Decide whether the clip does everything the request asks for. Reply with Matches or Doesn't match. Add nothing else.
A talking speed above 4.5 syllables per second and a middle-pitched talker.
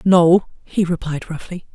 Doesn't match